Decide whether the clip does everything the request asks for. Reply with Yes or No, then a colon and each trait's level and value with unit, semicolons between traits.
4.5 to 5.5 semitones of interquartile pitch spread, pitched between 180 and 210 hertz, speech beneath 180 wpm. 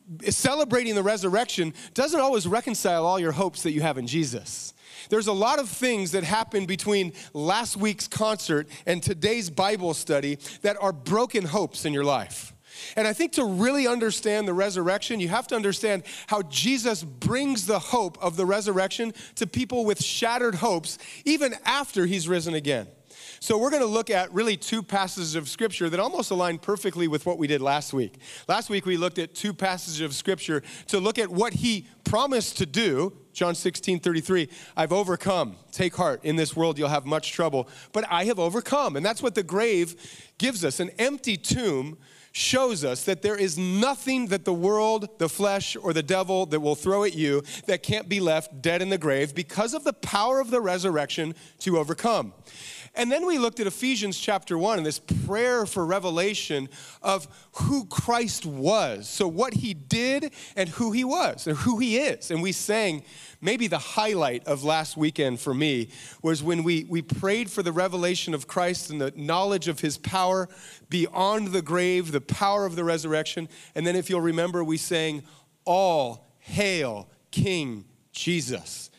No: average, 5.0 semitones; medium, 185 Hz; average, 185 wpm